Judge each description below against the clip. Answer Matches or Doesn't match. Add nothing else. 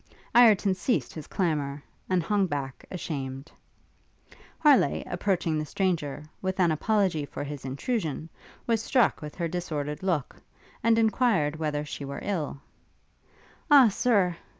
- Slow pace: Matches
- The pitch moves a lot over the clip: Matches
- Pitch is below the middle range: Doesn't match